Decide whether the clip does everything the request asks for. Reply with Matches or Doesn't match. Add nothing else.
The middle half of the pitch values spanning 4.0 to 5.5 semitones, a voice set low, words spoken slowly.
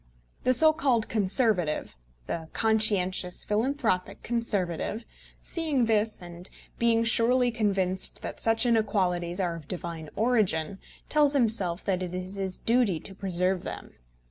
Doesn't match